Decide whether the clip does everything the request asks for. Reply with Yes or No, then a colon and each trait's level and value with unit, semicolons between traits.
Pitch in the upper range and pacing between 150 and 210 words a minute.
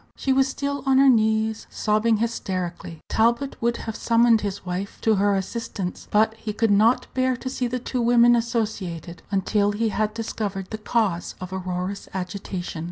Yes: high, 220 Hz; average, 170 wpm